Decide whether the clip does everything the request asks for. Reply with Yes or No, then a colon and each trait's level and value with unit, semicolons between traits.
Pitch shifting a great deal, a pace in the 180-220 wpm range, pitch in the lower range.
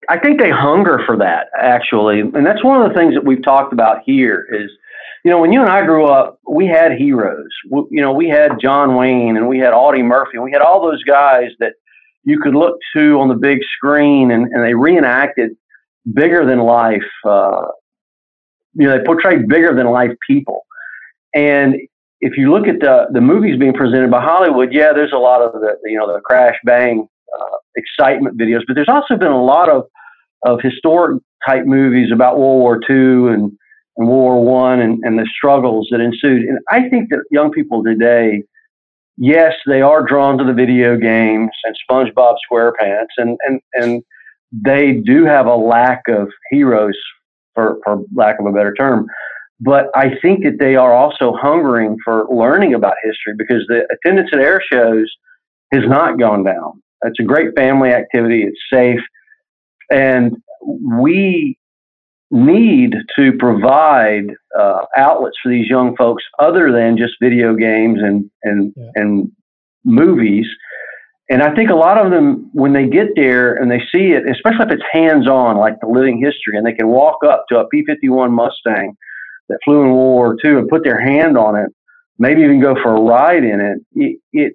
Yes: wide, 6.0 semitones; average, 185 wpm; low, 130 Hz